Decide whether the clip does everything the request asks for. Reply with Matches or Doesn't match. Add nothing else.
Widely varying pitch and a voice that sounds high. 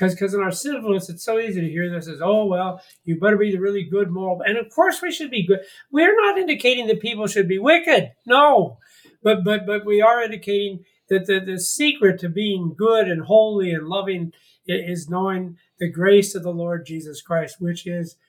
Doesn't match